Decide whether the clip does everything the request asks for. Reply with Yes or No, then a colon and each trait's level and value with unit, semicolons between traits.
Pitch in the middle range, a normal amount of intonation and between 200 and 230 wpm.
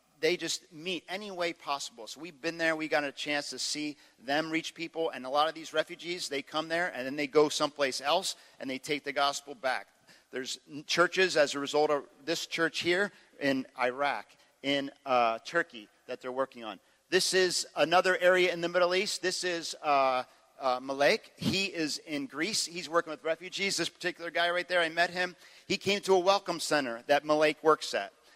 Yes: medium, 160 Hz; average, 3.9 semitones; fast, 205 wpm